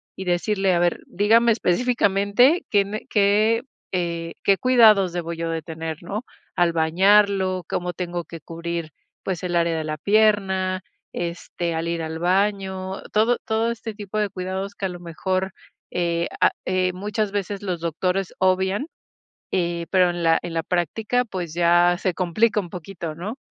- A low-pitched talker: No, medium, 185 Hz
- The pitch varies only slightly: No, average, 3.1 semitones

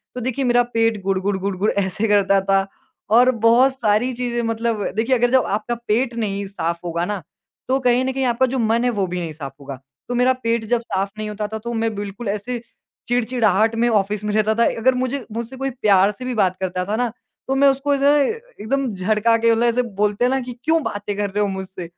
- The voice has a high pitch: Yes, high, 225 Hz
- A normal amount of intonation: Yes, average, 3.6 semitones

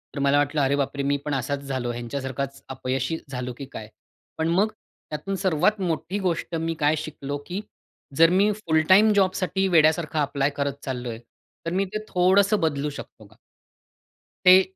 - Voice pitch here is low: No, medium, 150 Hz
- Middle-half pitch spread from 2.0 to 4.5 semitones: No, average, 4.9 semitones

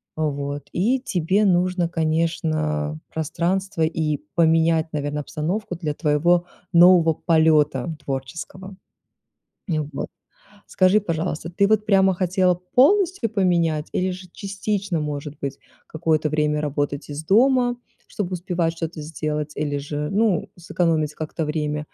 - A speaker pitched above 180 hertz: No, medium, 165 Hz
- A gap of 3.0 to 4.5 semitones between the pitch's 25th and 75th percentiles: Yes, average, 3.5 semitones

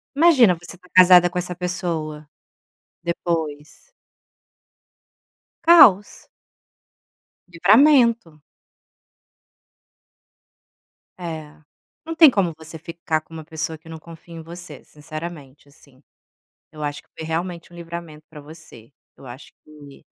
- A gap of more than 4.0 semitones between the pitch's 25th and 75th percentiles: No, average, 2.7 semitones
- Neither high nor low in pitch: Yes, medium, 165 Hz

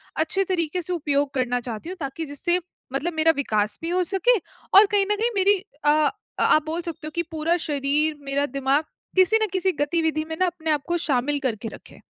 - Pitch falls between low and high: No, very high, 315 Hz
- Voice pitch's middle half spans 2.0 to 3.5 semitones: No, average, 3.9 semitones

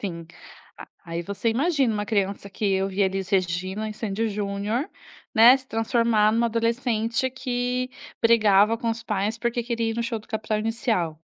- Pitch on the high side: Yes, high, 220 Hz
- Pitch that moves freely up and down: No, average, 2.7 semitones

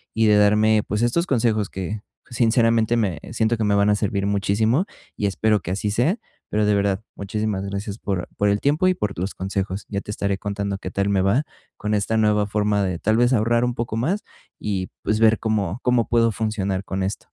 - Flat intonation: Yes, narrow, 2.2 semitones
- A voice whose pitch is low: Yes, low, 105 Hz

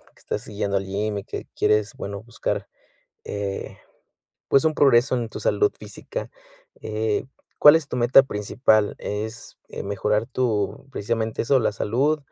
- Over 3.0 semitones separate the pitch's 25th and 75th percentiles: Yes, average, 3.8 semitones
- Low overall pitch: Yes, low, 110 Hz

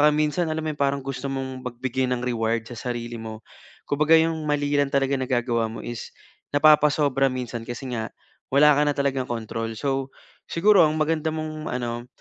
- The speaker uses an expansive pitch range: No, average, 3.8 semitones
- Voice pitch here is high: No, low, 135 Hz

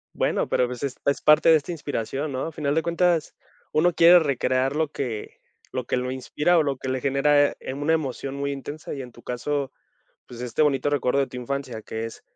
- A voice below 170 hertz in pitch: Yes, medium, 140 Hz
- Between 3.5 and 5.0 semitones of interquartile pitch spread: No, average, 2.8 semitones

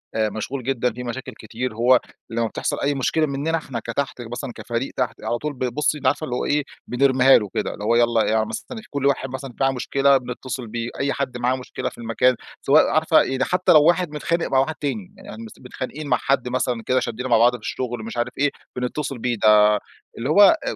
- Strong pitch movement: No, average, 2.9 semitones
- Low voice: Yes, low, 130 Hz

